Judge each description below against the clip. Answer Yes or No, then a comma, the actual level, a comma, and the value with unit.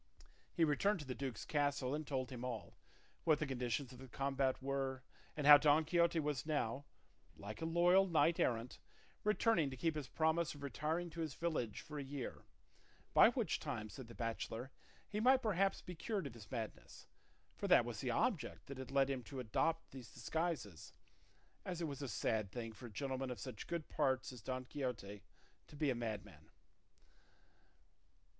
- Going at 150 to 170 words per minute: No, average, 185 wpm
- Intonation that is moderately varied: Yes, average, 4.4 semitones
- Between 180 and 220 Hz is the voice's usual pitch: No, medium, 140 Hz